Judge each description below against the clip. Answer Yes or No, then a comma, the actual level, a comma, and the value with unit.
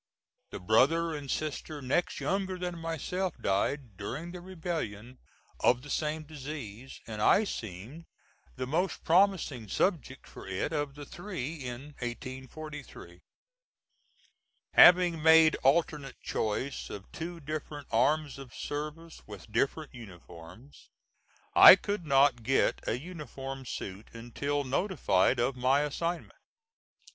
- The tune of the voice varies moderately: Yes, average, 5.0 semitones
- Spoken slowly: Yes, slow, 120 wpm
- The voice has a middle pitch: Yes, medium, 145 Hz